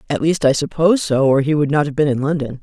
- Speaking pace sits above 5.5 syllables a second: Yes, 6.5 syllables/s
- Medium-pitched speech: Yes, medium, 150 Hz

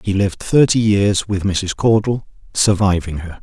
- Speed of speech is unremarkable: Yes, average, 160 wpm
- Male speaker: Yes, male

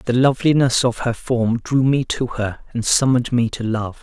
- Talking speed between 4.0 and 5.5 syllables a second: Yes, 4.9 syllables/s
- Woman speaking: No, male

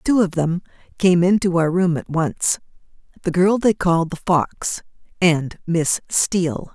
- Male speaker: No, female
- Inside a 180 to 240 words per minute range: No, average, 150 wpm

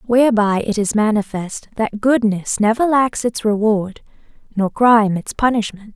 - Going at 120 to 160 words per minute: Yes, average, 140 wpm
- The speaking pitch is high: Yes, high, 220 Hz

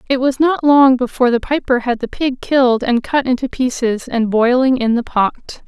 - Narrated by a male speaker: No, female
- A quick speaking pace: Yes, fast, 210 wpm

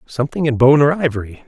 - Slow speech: No, fast, 205 wpm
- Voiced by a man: Yes, male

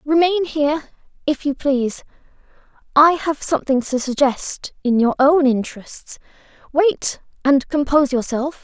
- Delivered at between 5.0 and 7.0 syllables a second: No, 4.6 syllables/s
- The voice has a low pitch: No, very high, 285 Hz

